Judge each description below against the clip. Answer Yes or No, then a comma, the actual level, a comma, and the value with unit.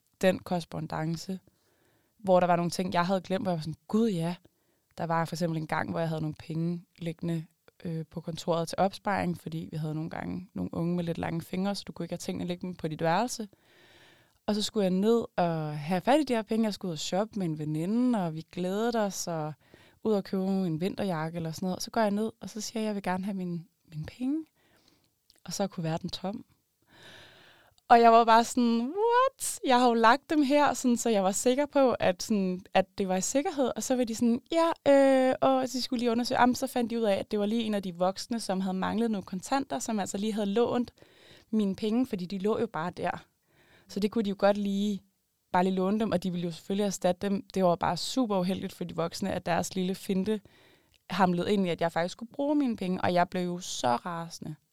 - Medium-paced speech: No, fast, 250 wpm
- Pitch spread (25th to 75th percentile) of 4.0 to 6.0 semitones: Yes, average, 4.8 semitones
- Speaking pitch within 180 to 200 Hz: Yes, high, 190 Hz